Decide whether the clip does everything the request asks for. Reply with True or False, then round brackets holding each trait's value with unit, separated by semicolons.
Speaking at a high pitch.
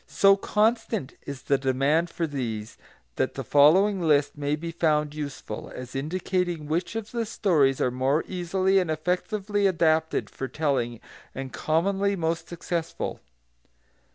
False (160 Hz)